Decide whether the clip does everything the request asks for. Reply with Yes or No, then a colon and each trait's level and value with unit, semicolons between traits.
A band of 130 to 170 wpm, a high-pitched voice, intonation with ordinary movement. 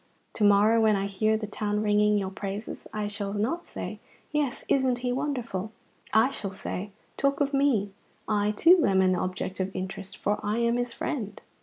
No: average, 185 wpm; high, 210 Hz; average, 3.5 semitones